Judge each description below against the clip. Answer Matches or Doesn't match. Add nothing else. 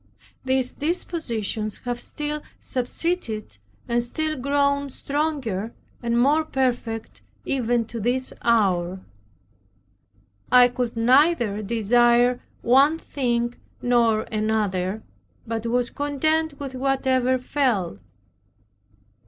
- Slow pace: Matches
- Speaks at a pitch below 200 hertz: Doesn't match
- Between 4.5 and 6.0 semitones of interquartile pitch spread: Doesn't match